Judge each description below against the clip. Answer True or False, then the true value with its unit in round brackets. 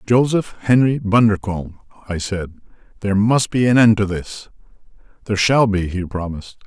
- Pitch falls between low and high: False (105 Hz)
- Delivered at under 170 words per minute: True (145 wpm)